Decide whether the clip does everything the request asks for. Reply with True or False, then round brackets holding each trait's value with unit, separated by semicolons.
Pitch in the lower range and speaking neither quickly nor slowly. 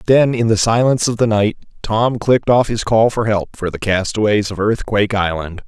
False (110 Hz; 210 wpm)